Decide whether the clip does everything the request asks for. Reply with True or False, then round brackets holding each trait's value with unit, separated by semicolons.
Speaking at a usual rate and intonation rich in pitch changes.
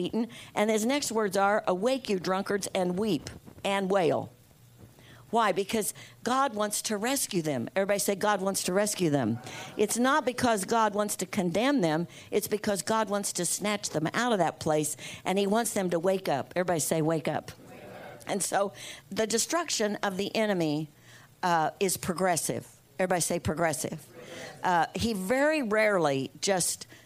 False (165 wpm; 4.9 semitones)